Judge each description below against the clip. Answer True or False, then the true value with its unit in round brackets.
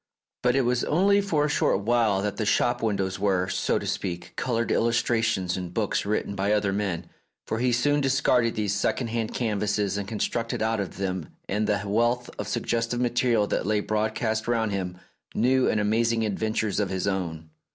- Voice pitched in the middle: False (110 Hz)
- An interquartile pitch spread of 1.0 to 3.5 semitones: True (3.1 semitones)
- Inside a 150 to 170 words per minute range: False (185 wpm)